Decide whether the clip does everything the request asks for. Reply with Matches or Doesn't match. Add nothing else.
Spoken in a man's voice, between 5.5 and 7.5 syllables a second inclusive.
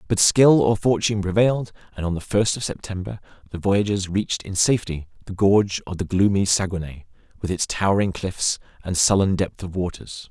Matches